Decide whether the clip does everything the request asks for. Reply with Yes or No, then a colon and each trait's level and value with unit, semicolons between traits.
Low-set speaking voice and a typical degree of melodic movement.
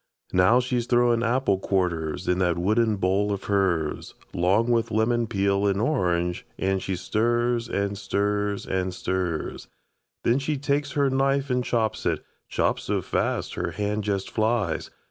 Yes: low, 105 Hz; average, 4.2 semitones